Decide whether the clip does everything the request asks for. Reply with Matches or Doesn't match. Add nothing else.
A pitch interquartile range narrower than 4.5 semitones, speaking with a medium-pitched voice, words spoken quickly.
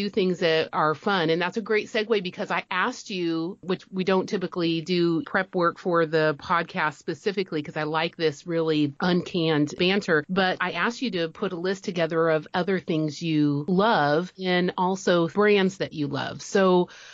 Doesn't match